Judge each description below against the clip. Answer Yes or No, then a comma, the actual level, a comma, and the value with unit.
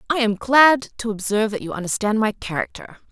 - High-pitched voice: Yes, high, 220 Hz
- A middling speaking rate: Yes, average, 195 wpm